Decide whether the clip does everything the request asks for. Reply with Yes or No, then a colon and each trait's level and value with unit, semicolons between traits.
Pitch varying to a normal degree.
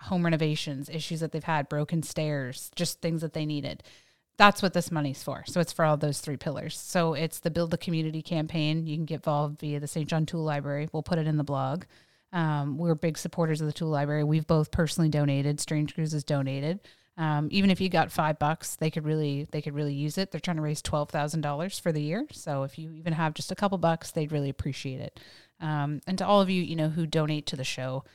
No: narrow, 2.0 semitones